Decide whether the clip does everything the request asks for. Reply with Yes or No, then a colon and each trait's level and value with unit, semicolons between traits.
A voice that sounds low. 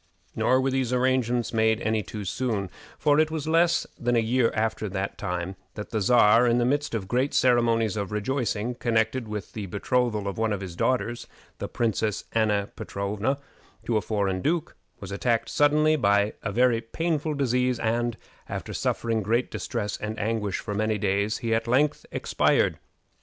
Yes: low, 115 Hz